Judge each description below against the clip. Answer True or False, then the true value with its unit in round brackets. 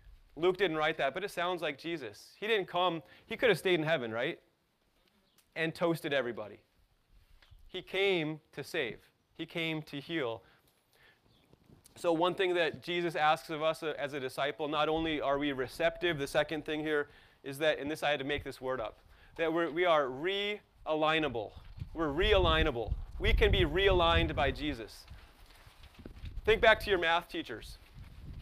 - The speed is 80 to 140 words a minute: False (170 wpm)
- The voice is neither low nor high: True (160 Hz)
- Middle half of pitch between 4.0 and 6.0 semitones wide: False (3.2 semitones)